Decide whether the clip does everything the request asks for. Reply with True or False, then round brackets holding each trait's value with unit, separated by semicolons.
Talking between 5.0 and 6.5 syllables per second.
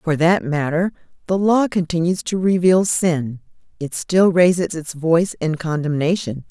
False (4.5 syllables/s)